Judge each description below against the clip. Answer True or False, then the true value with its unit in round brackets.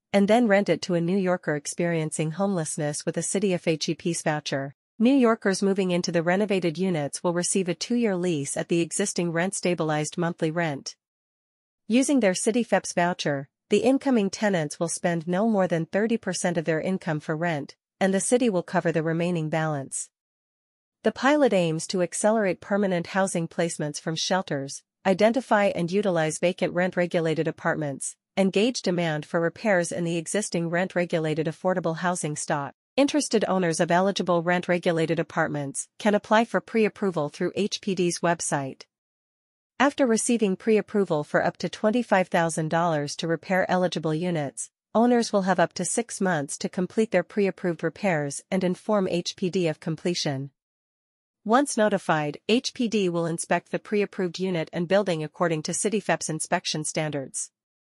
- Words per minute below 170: True (155 wpm)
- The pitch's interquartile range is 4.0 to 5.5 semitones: False (3.3 semitones)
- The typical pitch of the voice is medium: True (175 Hz)